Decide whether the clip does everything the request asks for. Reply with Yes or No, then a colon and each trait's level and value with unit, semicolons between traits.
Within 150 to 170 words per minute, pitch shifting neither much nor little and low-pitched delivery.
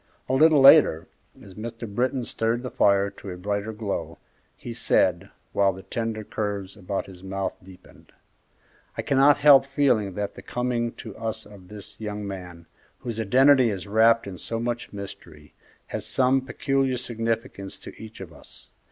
Yes: average, 165 wpm; average, 3.8 semitones; low, 110 Hz